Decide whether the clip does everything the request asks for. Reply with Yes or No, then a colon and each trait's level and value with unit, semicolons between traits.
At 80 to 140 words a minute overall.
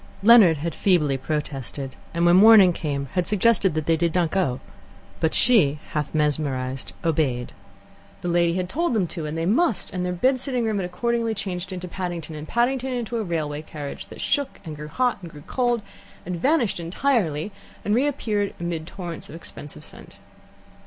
No: average, 185 wpm